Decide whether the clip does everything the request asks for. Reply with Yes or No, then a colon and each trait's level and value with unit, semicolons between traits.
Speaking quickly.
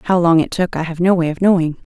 Yes: fast, 315 wpm